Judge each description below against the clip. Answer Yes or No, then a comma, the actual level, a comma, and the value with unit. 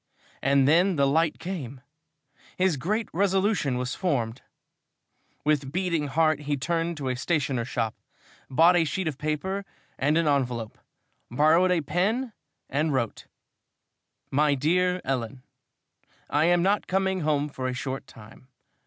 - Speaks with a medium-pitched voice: Yes, medium, 150 Hz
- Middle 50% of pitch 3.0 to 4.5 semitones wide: No, average, 5.0 semitones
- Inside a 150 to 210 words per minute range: No, average, 140 wpm